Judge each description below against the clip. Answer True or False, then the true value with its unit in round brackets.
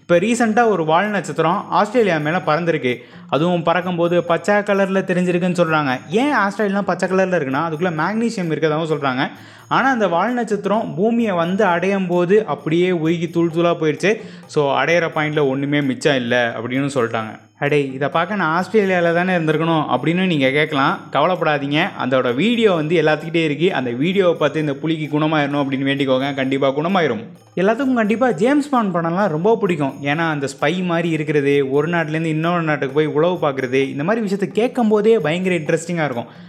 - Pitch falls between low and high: True (170 Hz)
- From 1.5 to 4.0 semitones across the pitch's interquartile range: False (4.4 semitones)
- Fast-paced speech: True (160 wpm)